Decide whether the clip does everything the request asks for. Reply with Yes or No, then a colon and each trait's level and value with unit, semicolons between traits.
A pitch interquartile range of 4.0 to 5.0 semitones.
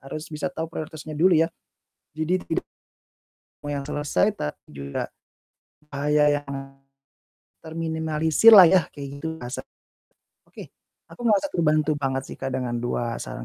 No: narrow, 2.6 semitones